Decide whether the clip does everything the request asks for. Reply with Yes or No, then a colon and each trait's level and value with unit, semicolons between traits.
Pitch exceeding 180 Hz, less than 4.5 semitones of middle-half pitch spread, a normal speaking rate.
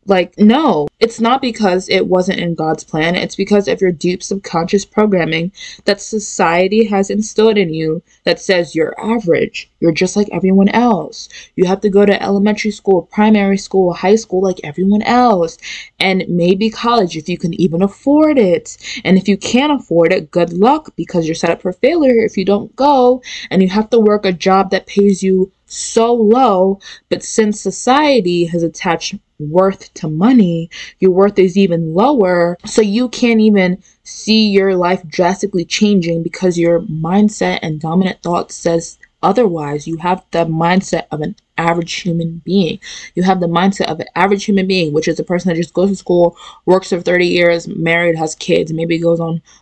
Yes: high, 190 Hz; average, 3.5 semitones; average, 185 wpm